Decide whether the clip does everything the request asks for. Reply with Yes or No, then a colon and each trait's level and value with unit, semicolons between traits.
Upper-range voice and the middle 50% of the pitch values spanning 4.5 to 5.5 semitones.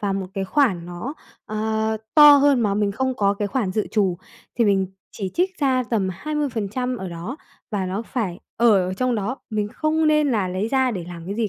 Yes: high, 215 Hz; average, 5.1 semitones